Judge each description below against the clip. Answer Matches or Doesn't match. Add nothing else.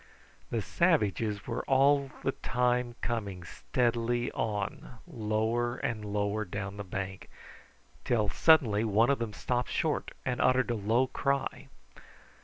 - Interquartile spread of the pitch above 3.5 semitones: Doesn't match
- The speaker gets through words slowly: Matches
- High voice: Doesn't match